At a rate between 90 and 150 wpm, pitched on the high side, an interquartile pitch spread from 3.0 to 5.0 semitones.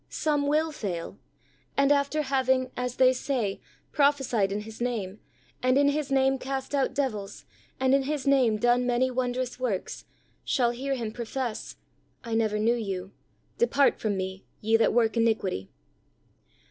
No: average, 160 wpm; very high, 250 Hz; average, 3.6 semitones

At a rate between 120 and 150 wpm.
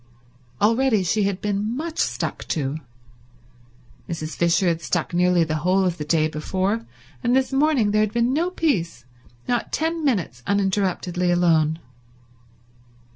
Yes: average, 140 wpm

